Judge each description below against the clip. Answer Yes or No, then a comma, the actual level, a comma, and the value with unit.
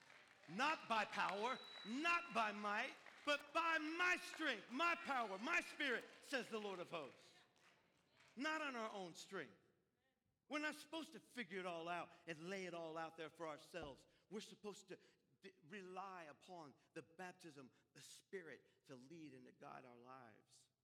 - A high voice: Yes, high, 195 Hz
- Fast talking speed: No, average, 165 wpm